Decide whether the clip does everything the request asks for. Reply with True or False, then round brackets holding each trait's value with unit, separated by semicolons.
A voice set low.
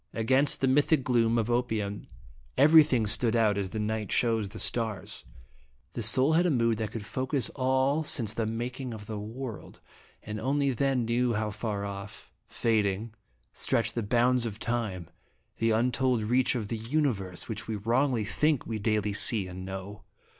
True (115 Hz)